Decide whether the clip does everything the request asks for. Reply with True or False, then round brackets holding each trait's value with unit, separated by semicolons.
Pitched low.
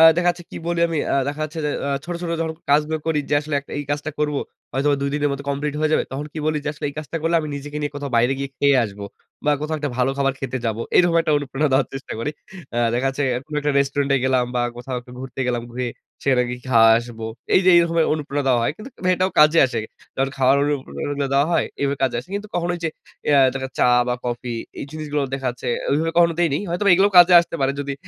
False (145 Hz)